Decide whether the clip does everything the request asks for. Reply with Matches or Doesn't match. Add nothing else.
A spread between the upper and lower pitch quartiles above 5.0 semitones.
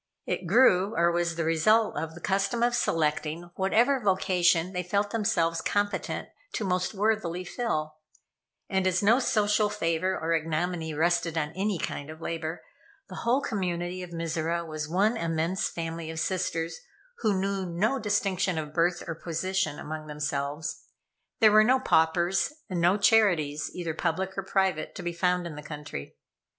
Doesn't match